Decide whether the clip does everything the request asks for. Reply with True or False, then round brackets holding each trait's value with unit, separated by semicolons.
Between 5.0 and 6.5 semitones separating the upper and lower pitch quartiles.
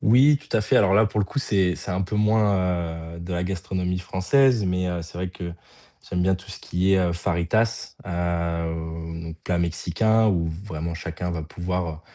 False (2.8 semitones)